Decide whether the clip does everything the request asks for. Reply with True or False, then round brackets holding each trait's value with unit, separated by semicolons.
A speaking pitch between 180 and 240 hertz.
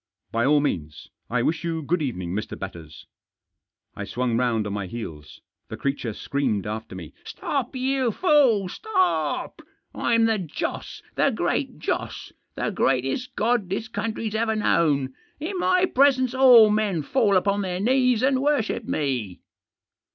True (185 Hz)